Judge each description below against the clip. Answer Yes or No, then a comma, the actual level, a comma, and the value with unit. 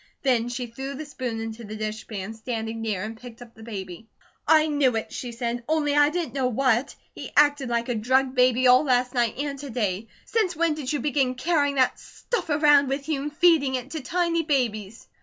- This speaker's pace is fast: Yes, fast, 215 wpm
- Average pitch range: Yes, average, 4.2 semitones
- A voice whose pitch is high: Yes, very high, 255 Hz